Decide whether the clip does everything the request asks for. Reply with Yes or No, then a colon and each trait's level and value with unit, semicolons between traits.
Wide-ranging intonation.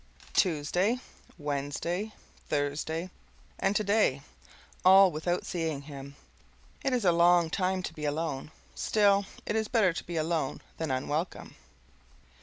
No: average, 4.6 semitones